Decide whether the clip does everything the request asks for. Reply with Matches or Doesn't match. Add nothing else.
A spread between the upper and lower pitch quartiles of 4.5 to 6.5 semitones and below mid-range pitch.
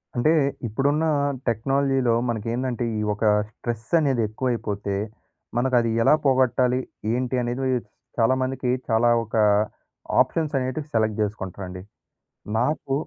Doesn't match